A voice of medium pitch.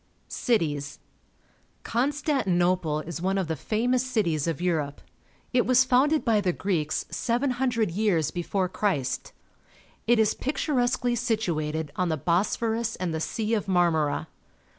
No: high, 195 Hz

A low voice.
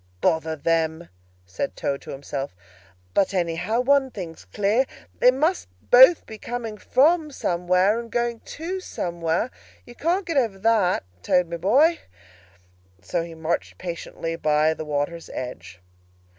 No: medium, 185 Hz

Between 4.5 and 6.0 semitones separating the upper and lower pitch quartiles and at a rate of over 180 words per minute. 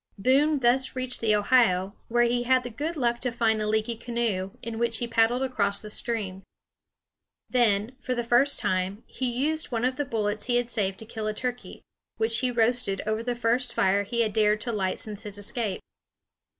No: average, 2.7 semitones; fast, 205 wpm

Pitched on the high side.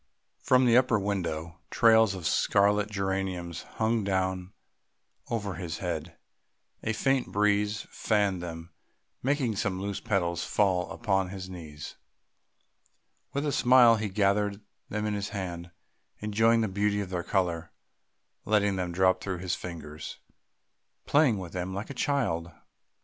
No: low, 100 Hz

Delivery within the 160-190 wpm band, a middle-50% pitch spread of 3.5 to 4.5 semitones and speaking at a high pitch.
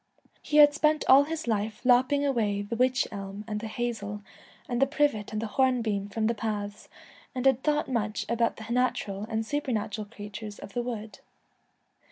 Yes: average, 185 wpm; average, 3.8 semitones; high, 230 Hz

